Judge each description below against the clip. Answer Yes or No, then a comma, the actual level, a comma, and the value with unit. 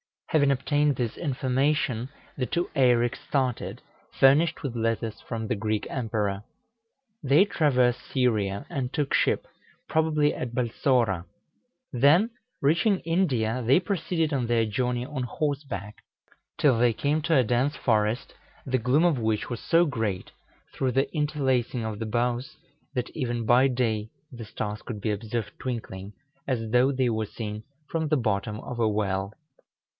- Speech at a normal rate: Yes, average, 150 wpm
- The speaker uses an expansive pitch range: No, average, 4.2 semitones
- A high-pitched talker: No, low, 125 Hz